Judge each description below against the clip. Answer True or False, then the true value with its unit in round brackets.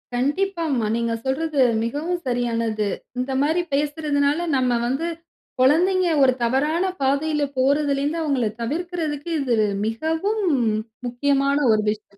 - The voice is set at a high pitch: True (285 Hz)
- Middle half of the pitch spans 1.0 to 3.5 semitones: False (4.2 semitones)